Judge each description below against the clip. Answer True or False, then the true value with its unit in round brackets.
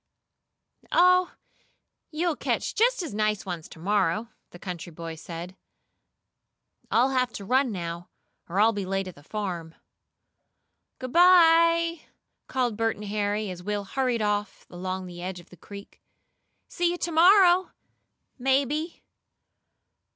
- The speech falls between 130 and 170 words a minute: True (135 wpm)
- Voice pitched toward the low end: False (210 Hz)